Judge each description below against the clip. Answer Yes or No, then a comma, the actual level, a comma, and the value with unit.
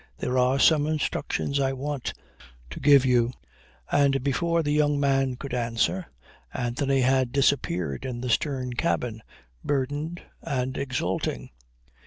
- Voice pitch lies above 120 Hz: Yes, low, 135 Hz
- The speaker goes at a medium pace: No, slow, 130 wpm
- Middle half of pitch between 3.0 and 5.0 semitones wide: No, narrow, 2.5 semitones